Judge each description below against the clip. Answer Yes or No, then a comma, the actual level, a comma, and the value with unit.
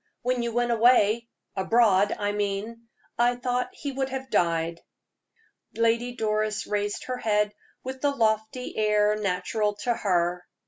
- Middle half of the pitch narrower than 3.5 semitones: Yes, average, 2.9 semitones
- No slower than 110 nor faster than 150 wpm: Yes, average, 140 wpm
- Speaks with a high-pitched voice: Yes, high, 220 Hz